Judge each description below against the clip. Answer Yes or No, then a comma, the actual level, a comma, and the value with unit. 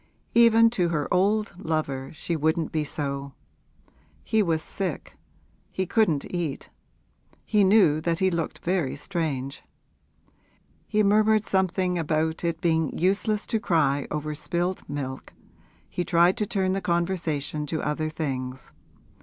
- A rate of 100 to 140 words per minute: Yes, slow, 135 wpm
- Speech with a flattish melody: No, average, 4.0 semitones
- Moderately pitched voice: Yes, medium, 170 Hz